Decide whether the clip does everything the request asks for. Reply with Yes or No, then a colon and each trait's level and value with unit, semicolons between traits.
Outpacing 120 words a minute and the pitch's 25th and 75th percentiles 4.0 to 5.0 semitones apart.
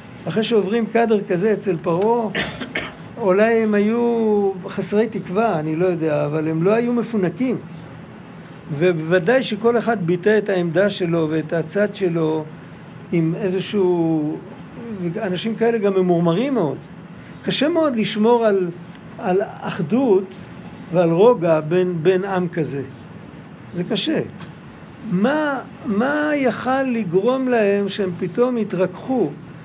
No: average, 115 wpm; average, 4.3 semitones